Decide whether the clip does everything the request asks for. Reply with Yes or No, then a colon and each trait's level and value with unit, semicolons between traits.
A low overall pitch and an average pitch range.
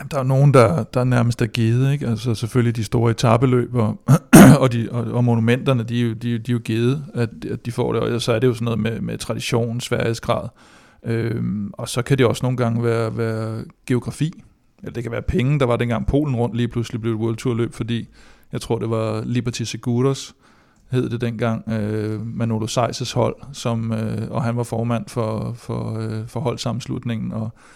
No: low, 120 Hz; narrow, 1.4 semitones